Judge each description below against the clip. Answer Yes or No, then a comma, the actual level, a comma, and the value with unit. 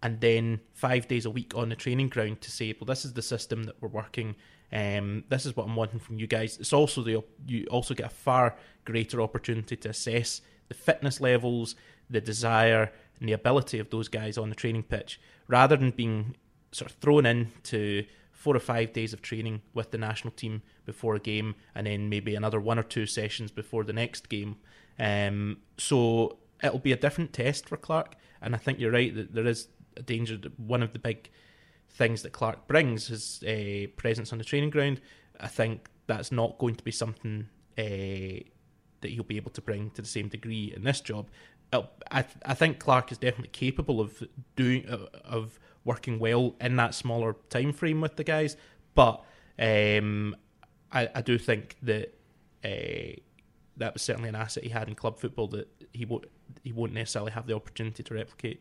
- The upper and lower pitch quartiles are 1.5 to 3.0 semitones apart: Yes, narrow, 2.4 semitones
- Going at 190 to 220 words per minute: Yes, average, 200 wpm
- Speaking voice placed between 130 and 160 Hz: No, low, 115 Hz